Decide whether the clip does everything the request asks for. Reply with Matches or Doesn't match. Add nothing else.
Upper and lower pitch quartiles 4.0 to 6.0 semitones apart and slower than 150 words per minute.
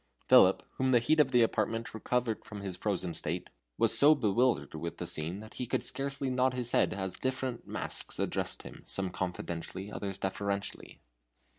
Doesn't match